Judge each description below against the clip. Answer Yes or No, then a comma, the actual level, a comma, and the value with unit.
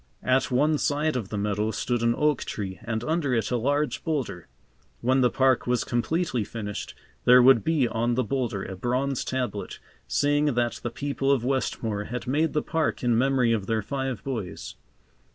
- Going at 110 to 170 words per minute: No, average, 185 wpm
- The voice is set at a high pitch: No, low, 125 Hz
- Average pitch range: Yes, average, 3.4 semitones